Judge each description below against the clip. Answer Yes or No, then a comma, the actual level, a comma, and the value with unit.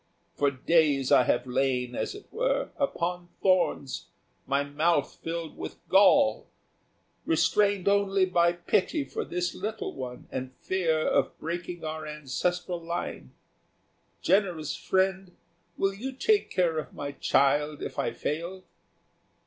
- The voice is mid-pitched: Yes, medium, 170 Hz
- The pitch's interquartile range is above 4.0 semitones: Yes, average, 4.8 semitones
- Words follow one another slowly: Yes, slow, 130 wpm